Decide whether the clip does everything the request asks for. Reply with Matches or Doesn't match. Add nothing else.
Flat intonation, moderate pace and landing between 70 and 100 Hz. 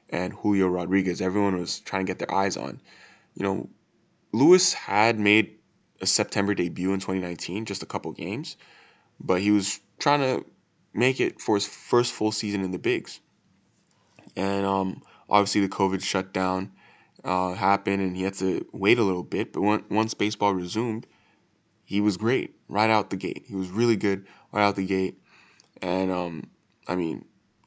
Matches